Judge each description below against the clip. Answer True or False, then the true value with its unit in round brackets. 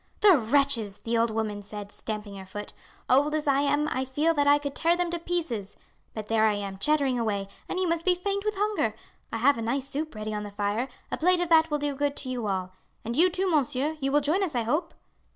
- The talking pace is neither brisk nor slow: False (250 wpm)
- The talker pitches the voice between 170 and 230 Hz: False (275 Hz)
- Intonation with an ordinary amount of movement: False (6.6 semitones)